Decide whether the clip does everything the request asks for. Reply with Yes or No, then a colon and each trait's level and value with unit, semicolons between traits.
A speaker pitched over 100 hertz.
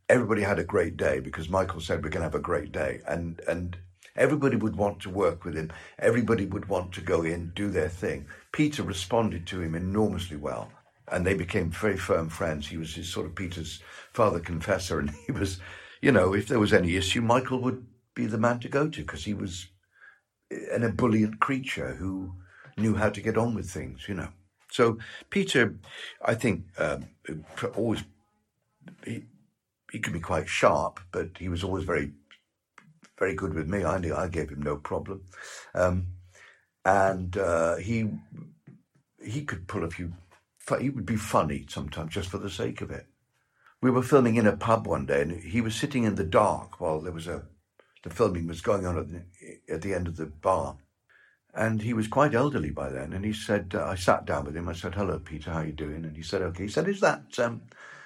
No: very low, 95 Hz